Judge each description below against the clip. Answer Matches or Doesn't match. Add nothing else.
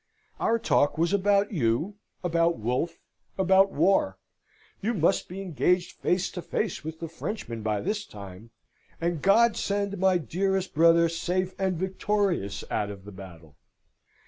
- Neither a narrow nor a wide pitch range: Doesn't match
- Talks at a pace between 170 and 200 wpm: Doesn't match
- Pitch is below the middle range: Doesn't match